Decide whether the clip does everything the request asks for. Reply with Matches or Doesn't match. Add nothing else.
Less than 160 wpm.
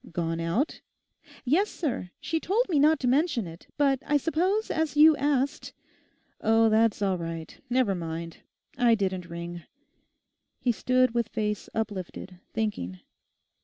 Matches